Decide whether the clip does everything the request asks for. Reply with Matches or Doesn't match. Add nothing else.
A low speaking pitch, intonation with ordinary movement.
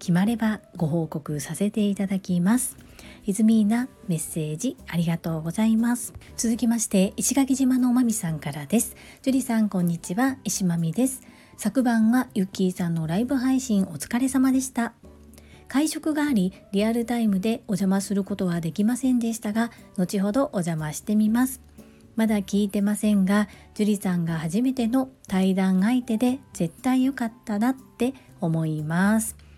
Doesn't match